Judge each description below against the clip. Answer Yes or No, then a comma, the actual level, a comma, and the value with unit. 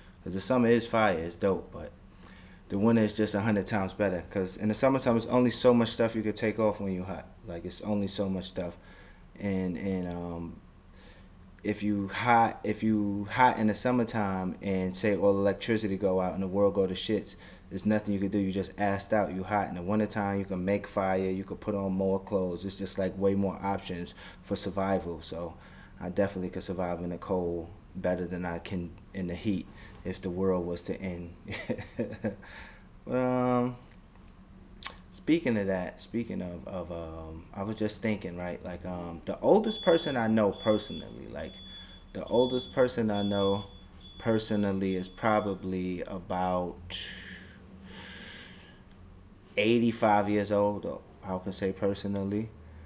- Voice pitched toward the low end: Yes, very low, 95 Hz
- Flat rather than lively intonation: Yes, narrow, 2.3 semitones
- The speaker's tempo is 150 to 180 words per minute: Yes, average, 175 wpm